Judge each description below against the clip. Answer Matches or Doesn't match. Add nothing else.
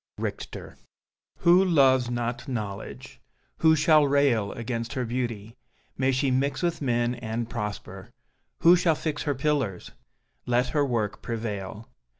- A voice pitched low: Matches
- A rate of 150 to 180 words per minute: Doesn't match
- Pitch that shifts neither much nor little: Matches